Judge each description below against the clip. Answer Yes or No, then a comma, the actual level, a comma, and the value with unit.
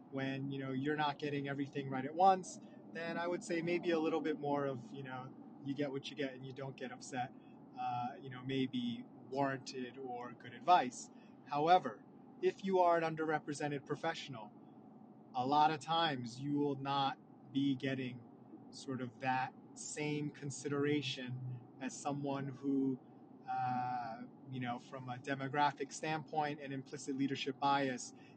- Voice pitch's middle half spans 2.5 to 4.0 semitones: Yes, average, 3.2 semitones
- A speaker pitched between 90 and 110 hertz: No, medium, 140 Hz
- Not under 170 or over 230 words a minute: No, average, 160 wpm